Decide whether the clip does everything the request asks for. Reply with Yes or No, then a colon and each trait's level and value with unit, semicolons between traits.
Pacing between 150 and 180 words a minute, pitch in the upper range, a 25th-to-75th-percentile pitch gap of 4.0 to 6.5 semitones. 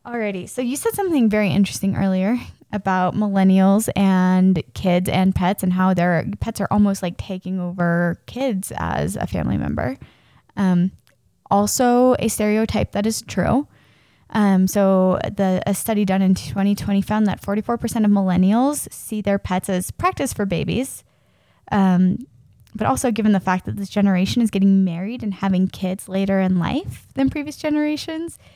No: average, 160 wpm; high, 195 Hz; average, 3.1 semitones